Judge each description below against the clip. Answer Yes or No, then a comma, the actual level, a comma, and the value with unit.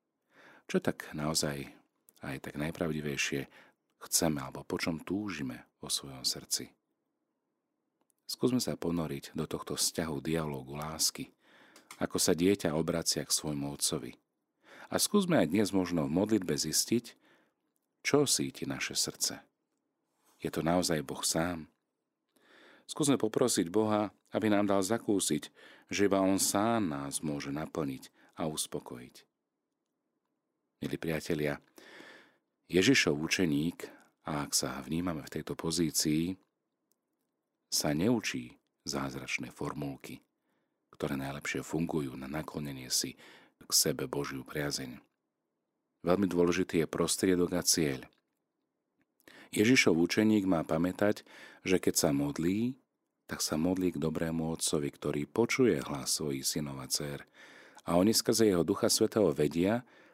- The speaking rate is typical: Yes, average, 120 wpm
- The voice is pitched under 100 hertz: Yes, very low, 80 Hz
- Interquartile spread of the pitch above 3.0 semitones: Yes, average, 4.8 semitones